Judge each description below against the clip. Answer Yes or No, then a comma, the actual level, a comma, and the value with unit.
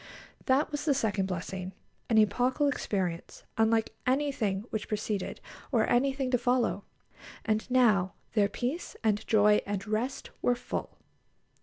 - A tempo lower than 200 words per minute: Yes, slow, 135 wpm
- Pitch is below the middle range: No, high, 220 Hz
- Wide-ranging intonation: No, average, 3.9 semitones